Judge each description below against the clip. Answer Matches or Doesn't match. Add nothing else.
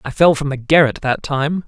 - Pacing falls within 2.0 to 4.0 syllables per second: Doesn't match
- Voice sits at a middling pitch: Matches